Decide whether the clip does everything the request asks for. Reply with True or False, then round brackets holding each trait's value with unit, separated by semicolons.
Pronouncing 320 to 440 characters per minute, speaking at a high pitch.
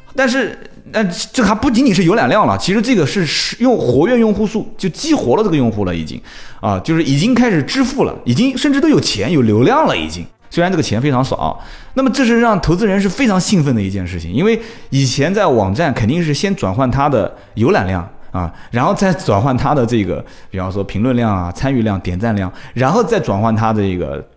False (330 characters per minute; 150 Hz)